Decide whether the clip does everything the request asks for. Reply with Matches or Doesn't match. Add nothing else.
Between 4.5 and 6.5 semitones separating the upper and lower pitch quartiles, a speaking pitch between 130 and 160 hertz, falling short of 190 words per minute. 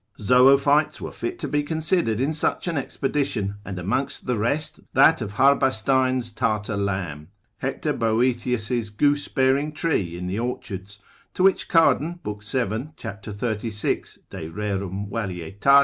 Doesn't match